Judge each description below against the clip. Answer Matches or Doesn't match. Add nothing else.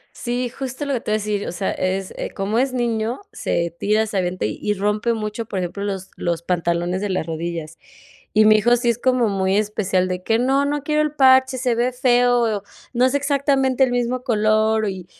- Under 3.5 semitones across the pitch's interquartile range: Doesn't match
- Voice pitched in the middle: Doesn't match